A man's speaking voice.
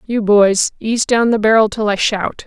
No: female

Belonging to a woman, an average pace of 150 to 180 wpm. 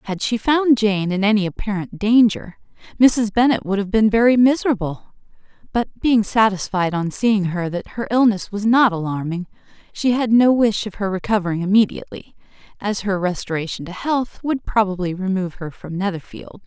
Yes: female; average, 165 wpm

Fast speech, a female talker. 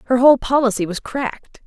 No: average, 180 wpm; female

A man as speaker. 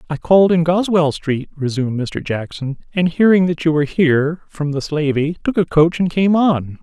Yes: male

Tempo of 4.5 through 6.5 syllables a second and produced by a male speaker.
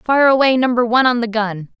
No: 5.8 syllables/s; female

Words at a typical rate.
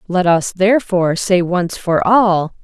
Yes: average, 160 wpm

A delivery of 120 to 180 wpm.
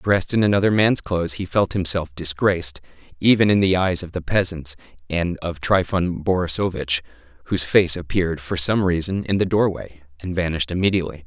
Yes: average, 170 wpm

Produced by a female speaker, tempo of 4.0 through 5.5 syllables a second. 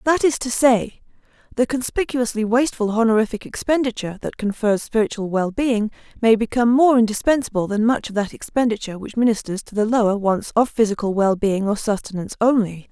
No: female; 5.9 syllables/s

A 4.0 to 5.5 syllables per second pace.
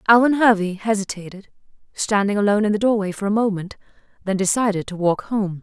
No: 6.1 syllables/s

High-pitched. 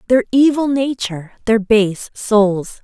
Yes: high, 225 Hz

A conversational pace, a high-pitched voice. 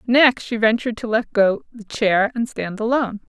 Yes: average, 195 wpm; high, 225 Hz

